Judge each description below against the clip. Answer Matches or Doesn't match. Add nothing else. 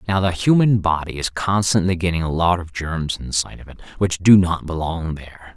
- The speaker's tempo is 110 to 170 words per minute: Doesn't match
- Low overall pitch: Matches